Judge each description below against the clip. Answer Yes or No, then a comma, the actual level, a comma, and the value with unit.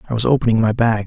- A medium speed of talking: No, fast, 280 wpm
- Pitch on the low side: Yes, low, 115 Hz